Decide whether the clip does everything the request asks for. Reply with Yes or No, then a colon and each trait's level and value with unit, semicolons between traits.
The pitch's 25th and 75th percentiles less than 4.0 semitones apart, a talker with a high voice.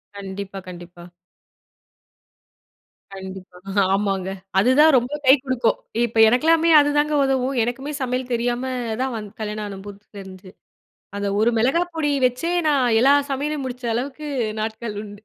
No: average, 5.1 semitones; high, 240 Hz